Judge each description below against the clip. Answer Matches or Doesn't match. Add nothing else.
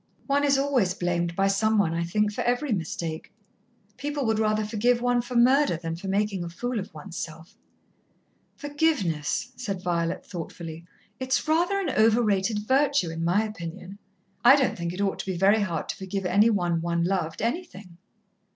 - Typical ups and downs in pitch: Doesn't match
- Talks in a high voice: Matches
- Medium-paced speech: Matches